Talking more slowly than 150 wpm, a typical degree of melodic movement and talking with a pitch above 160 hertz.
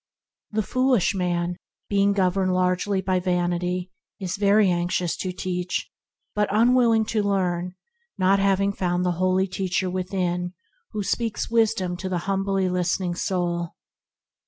No: slow, 135 wpm; narrow, 1.9 semitones; medium, 185 Hz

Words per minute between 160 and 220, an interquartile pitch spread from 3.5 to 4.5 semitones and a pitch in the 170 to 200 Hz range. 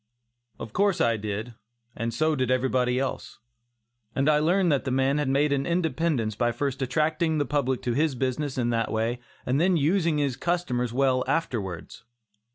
No: average, 175 wpm; average, 3.9 semitones; low, 135 Hz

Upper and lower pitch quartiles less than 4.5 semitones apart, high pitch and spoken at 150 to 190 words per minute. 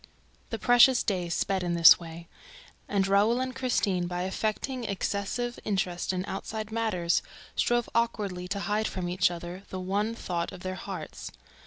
Yes: average, 3.9 semitones; high, 195 Hz; average, 160 wpm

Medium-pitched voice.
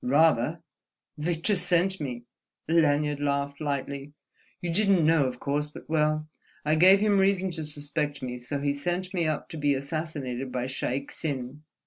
Yes: medium, 150 Hz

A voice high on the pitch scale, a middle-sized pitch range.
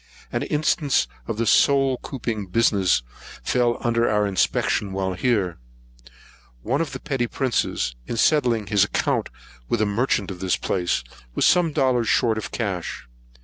No: low, 115 Hz; average, 4.4 semitones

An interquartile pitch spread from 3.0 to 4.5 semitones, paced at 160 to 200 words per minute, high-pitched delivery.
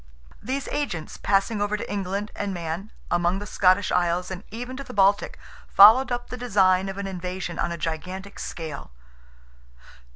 No: narrow, 2.6 semitones; average, 165 wpm; high, 195 Hz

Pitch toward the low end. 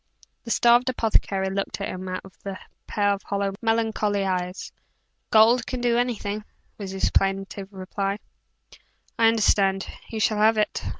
No: high, 205 Hz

